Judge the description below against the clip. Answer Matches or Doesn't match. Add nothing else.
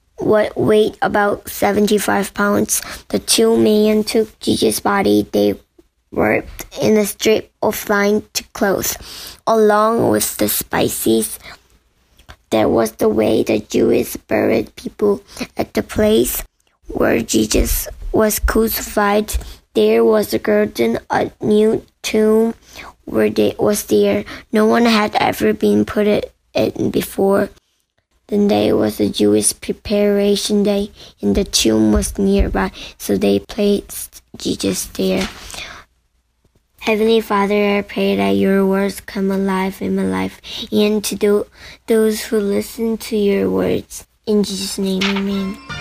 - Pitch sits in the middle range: Doesn't match